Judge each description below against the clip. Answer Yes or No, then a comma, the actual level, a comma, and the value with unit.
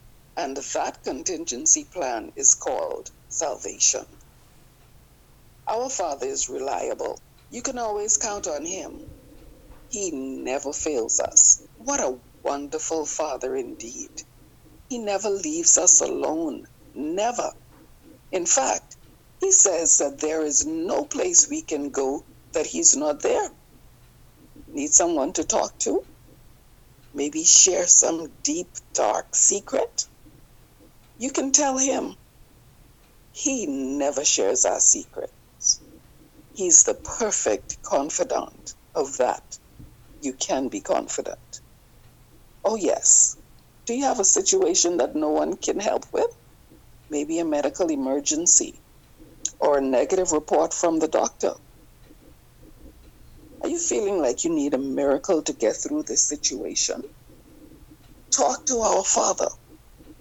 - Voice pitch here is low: No, very high, 290 Hz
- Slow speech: Yes, slow, 120 wpm